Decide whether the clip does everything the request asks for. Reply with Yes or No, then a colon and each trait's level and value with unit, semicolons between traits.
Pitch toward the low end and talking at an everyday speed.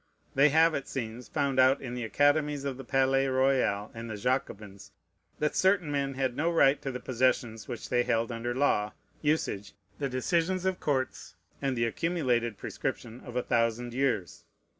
Yes: low, 130 Hz; average, 175 wpm